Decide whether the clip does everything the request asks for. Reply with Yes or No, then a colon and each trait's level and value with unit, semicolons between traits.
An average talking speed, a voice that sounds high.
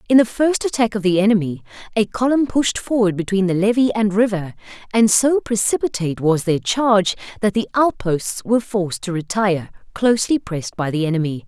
Yes: average, 180 wpm; high, 205 Hz